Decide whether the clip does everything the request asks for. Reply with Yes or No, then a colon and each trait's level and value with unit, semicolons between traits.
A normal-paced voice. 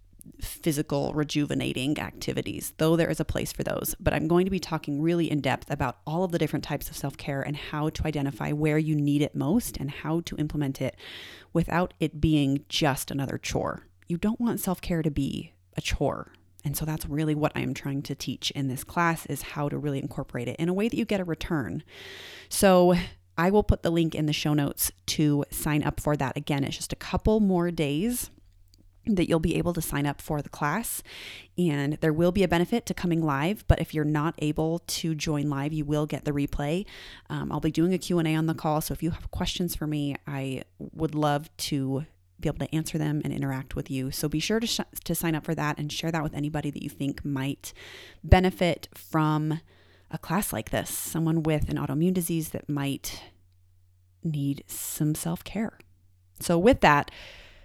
No: fast, 215 wpm